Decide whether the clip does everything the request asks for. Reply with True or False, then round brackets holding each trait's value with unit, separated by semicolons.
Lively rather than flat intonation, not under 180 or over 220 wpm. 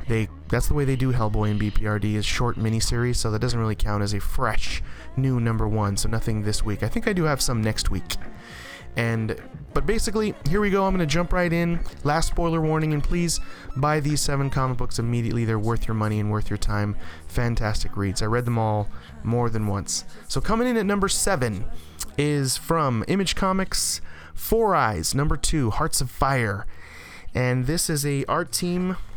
True (6.4 semitones; 200 wpm)